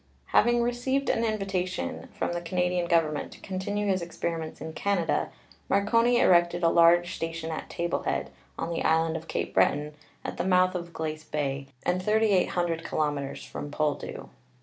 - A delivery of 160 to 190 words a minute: Yes, average, 170 wpm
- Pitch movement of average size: Yes, average, 3.1 semitones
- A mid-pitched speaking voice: Yes, medium, 175 Hz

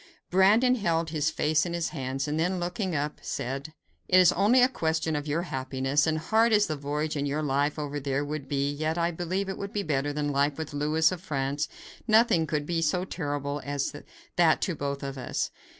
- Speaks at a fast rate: Yes, fast, 215 wpm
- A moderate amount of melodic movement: Yes, average, 3.5 semitones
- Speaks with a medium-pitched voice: Yes, medium, 155 Hz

